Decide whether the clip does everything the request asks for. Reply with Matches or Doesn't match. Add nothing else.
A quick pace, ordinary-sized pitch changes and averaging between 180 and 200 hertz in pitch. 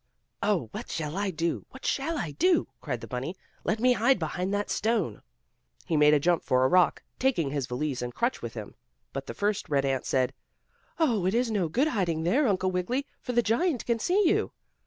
Doesn't match